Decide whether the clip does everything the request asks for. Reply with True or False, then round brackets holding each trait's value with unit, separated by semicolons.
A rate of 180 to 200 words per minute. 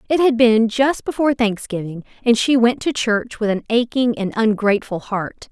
True (185 wpm)